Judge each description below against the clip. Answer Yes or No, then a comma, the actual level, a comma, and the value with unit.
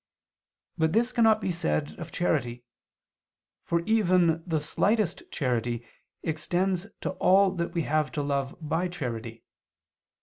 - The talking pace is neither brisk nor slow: No, slow, 130 wpm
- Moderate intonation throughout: Yes, average, 4.3 semitones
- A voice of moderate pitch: Yes, medium, 165 Hz